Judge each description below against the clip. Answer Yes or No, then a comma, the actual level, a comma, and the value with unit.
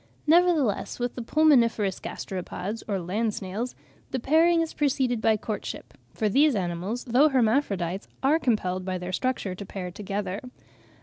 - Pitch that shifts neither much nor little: No, wide, 5.7 semitones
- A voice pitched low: No, high, 225 Hz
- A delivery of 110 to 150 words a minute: Yes, average, 145 wpm